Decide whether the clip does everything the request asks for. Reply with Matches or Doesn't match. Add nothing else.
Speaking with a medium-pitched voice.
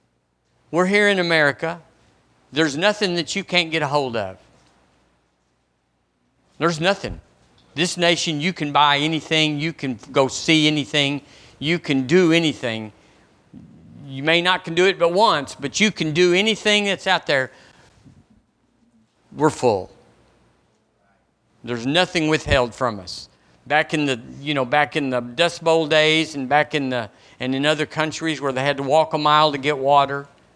Matches